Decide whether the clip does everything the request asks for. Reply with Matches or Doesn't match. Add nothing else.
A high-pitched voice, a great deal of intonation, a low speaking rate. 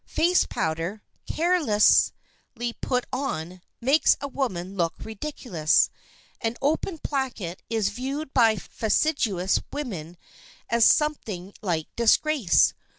Matches